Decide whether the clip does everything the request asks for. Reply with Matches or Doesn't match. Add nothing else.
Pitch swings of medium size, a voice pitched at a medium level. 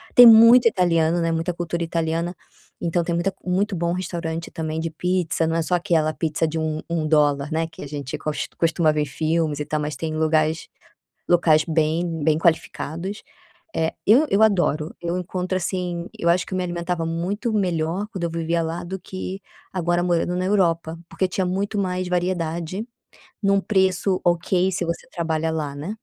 Doesn't match